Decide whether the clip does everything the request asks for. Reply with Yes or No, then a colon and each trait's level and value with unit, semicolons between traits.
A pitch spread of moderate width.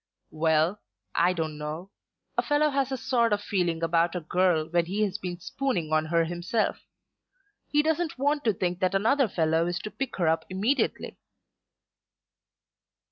No: wide, 5.9 semitones